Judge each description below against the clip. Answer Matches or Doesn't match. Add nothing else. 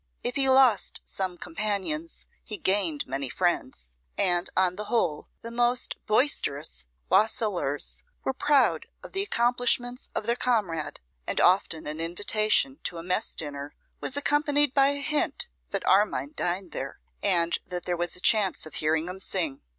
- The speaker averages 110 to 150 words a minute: Doesn't match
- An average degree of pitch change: Doesn't match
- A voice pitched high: Matches